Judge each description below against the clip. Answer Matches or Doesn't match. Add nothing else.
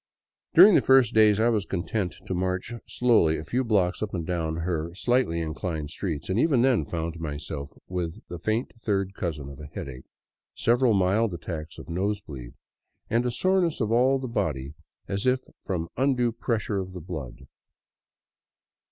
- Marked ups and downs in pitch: Matches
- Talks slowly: Doesn't match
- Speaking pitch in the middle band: Doesn't match